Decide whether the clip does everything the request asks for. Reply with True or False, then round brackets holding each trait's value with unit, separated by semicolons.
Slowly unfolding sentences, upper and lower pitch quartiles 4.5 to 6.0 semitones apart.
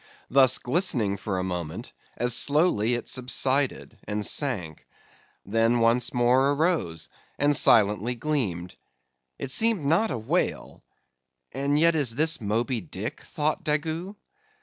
True (125 wpm; 5.6 semitones)